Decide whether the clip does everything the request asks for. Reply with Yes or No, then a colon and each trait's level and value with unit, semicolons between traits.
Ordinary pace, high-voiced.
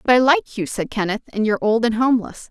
No: fast, 265 wpm; high, 225 Hz